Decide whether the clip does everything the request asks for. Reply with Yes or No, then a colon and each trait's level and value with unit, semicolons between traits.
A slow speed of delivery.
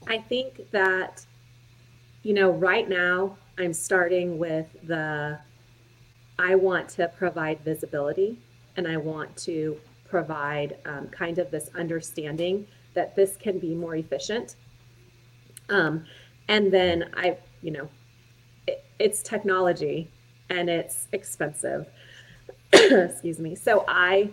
Yes: slow, 120 wpm